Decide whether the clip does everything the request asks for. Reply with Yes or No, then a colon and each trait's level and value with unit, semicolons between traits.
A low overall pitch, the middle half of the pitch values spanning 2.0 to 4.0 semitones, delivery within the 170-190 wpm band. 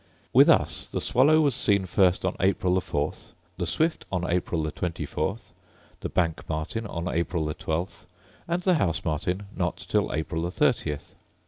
Yes: very low, 90 Hz; average, 3.7 semitones; average, 175 wpm